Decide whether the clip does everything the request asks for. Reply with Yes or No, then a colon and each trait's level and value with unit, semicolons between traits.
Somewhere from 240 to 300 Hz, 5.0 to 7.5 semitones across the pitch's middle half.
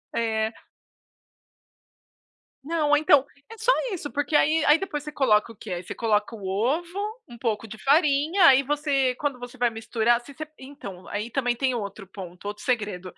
Yes: very high, 250 Hz; average, 5.3 semitones